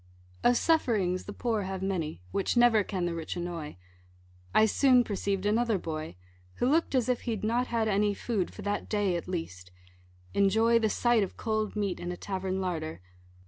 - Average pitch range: Yes, average, 4.1 semitones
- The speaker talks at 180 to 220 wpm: Yes, average, 185 wpm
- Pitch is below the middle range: No, high, 205 Hz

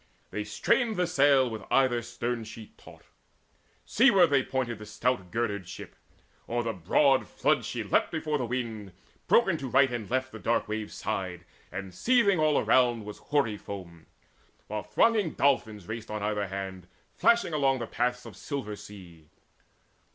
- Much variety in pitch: No, average, 4.8 semitones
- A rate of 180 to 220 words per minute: No, average, 165 wpm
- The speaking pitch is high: No, low, 120 Hz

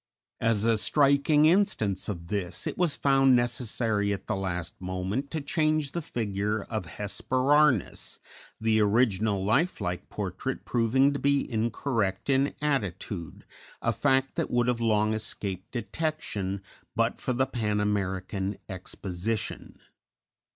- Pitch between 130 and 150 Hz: No, low, 110 Hz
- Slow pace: Yes, slow, 130 wpm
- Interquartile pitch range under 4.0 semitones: No, wide, 5.4 semitones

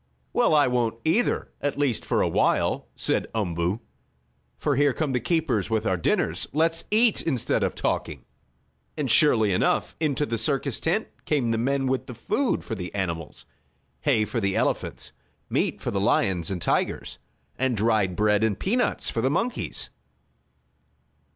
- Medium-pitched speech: No, low, 125 Hz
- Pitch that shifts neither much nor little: No, wide, 5.8 semitones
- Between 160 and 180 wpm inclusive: Yes, average, 165 wpm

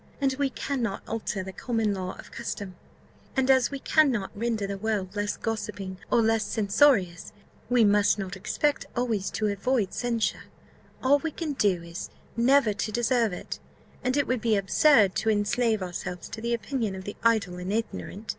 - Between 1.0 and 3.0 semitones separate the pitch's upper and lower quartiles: No, average, 3.9 semitones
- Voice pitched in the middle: No, high, 220 Hz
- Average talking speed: Yes, average, 175 wpm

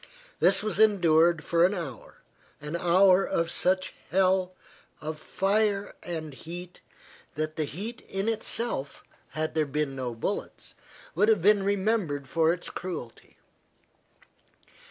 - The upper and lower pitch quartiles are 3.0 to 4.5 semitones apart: Yes, average, 4.1 semitones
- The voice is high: No, medium, 175 Hz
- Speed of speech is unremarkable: No, slow, 130 wpm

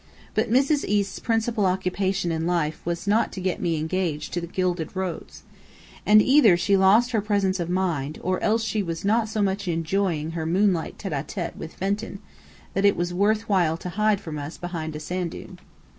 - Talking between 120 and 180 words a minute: No, average, 200 wpm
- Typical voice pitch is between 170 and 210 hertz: Yes, medium, 185 Hz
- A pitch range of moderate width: Yes, average, 3.6 semitones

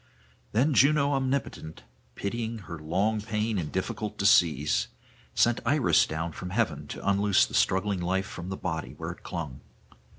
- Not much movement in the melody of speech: No, average, 5.3 semitones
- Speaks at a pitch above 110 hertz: No, low, 100 Hz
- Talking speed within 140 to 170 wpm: Yes, average, 155 wpm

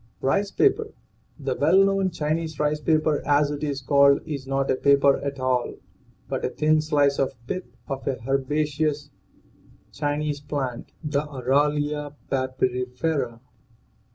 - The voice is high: No, medium, 145 Hz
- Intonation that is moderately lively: No, narrow, 1.9 semitones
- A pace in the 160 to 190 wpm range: No, average, 140 wpm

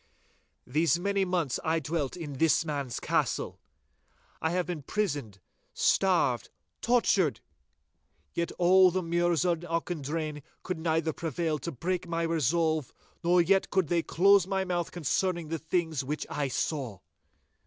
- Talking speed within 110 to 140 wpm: Yes, slow, 135 wpm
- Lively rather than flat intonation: No, average, 2.9 semitones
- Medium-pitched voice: Yes, medium, 165 Hz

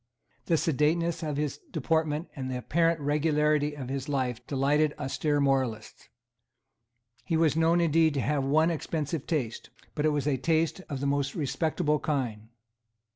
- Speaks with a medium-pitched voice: Yes, medium, 150 Hz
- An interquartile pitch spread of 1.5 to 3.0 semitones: Yes, average, 2.7 semitones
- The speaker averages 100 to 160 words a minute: Yes, average, 155 wpm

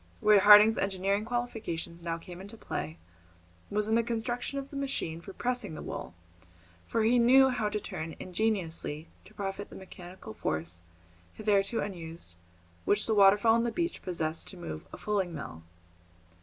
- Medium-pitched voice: No, high, 200 Hz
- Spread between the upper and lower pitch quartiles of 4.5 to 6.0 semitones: Yes, average, 4.8 semitones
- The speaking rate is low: No, average, 165 wpm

